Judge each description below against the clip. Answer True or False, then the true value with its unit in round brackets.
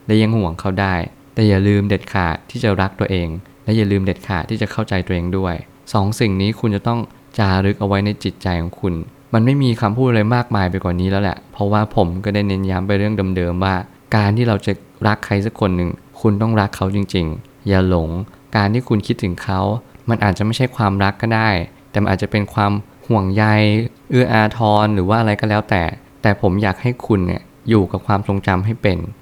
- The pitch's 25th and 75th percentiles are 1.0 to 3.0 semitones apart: True (2.6 semitones)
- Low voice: True (100 Hz)